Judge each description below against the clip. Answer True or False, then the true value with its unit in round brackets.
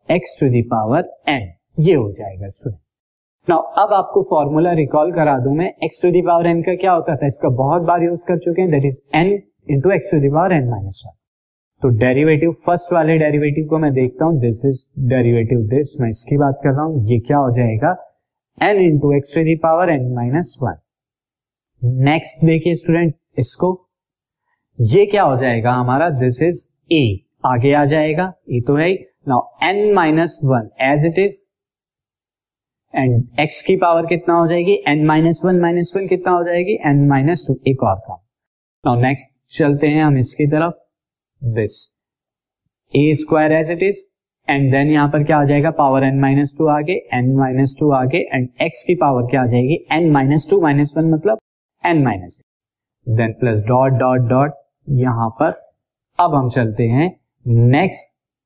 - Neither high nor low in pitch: True (145 Hz)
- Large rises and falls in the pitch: False (4.7 semitones)